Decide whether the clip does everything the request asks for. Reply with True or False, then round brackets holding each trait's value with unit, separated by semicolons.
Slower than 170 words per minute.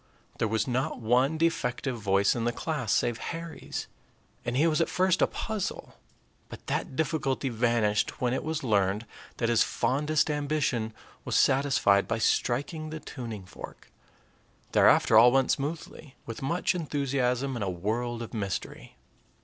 True (150 wpm)